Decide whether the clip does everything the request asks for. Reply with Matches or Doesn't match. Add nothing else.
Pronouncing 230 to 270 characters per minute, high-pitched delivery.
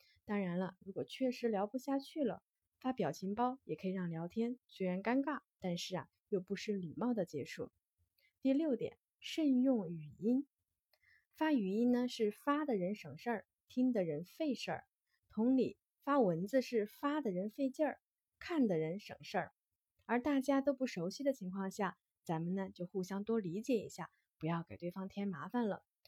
Matches